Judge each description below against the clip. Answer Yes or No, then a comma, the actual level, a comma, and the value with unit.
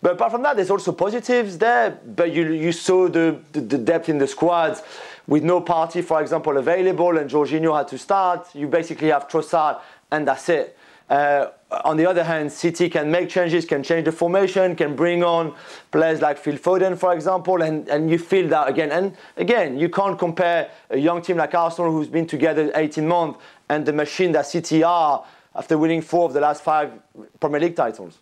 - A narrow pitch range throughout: Yes, narrow, 2.3 semitones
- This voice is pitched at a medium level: Yes, medium, 165 Hz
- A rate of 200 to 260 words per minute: Yes, fast, 205 wpm